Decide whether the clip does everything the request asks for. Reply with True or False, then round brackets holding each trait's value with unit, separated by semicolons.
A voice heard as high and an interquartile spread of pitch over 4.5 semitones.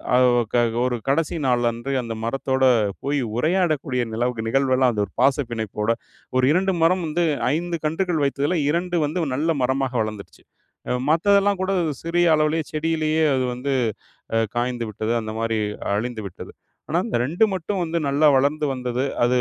False (140 Hz; 5.1 semitones)